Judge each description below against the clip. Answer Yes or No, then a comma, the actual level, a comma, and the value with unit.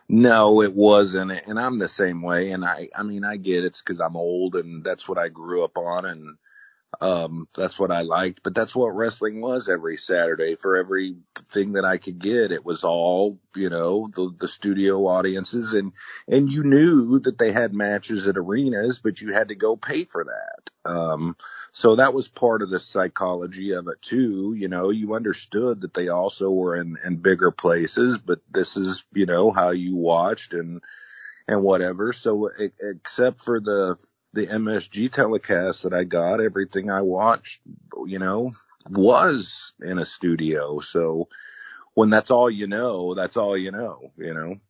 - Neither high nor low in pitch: No, very low, 95 Hz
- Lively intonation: No, average, 3.5 semitones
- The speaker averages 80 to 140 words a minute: No, average, 185 wpm